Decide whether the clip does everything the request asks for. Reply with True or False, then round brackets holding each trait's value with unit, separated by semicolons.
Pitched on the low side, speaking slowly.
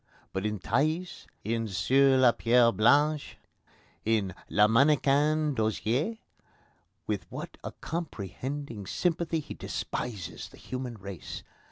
True (125 Hz; 115 wpm)